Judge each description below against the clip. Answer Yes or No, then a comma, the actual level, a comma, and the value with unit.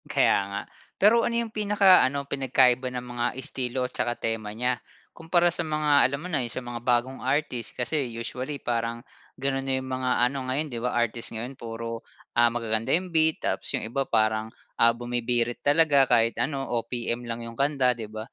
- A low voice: Yes, low, 125 Hz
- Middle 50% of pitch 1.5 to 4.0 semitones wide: Yes, average, 3.2 semitones